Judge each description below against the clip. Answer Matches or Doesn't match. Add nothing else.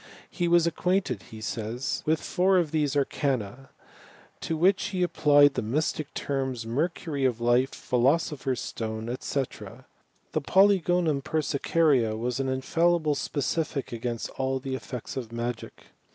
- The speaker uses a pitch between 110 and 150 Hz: Matches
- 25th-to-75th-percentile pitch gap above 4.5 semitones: Matches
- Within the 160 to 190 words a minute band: Doesn't match